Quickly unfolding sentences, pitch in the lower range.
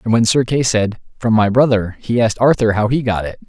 Yes: fast, 260 wpm; low, 115 Hz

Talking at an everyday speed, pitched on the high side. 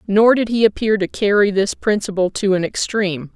Yes: average, 195 wpm; high, 205 Hz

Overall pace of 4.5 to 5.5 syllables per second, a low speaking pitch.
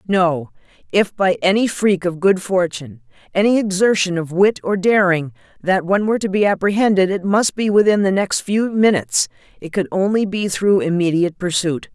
No: 5.3 syllables/s; high, 190 Hz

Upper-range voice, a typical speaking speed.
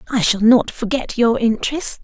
Yes: high, 230 Hz; average, 175 wpm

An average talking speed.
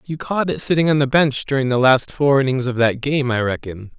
No: fast, 255 wpm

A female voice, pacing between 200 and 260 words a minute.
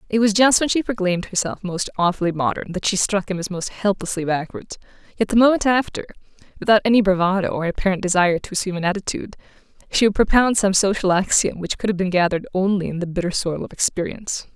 Yes: female; fast, 205 wpm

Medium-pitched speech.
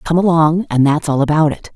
Yes: medium, 155 Hz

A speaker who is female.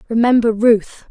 Yes: female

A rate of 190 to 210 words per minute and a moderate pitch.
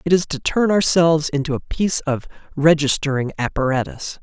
No: average, 155 wpm; medium, 155 Hz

